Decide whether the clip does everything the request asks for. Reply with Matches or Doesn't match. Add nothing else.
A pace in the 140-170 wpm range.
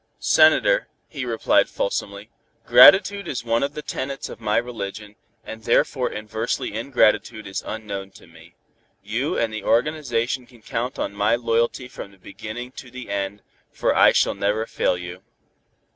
Matches